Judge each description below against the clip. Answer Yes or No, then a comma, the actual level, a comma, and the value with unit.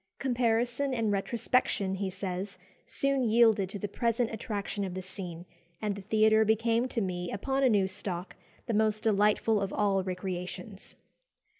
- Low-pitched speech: No, high, 210 Hz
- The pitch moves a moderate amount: Yes, average, 3.1 semitones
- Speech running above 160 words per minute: No, average, 155 wpm